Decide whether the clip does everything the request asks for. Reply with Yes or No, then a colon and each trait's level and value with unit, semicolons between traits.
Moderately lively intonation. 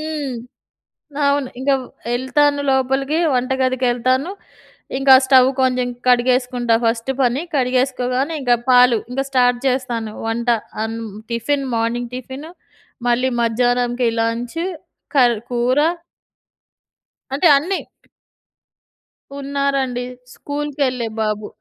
No: narrow, 2.0 semitones